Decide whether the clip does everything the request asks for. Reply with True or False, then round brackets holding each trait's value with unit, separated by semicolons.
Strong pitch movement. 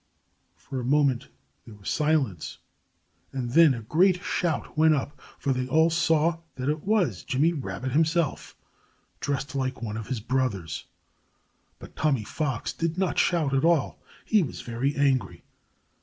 False (4.0 semitones)